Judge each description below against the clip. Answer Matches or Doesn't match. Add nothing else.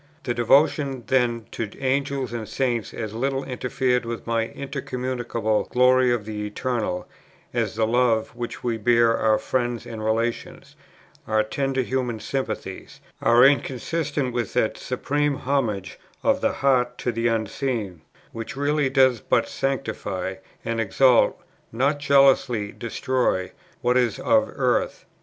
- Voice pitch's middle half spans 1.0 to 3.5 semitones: Matches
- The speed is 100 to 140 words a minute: Matches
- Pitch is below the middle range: Matches